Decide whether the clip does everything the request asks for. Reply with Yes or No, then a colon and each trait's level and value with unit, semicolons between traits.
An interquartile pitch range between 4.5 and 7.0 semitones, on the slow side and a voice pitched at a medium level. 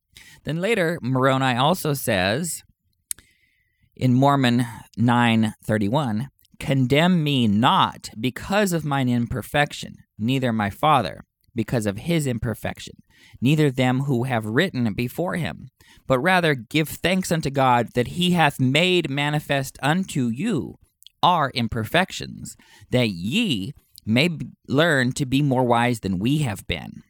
No: average, 4.8 semitones; slow, 125 wpm; low, 130 Hz